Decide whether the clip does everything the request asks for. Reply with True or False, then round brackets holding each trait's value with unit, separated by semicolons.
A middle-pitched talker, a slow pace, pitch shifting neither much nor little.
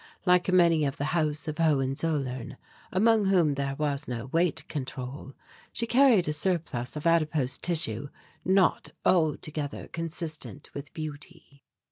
True (155 Hz; 130 wpm; 3.6 semitones)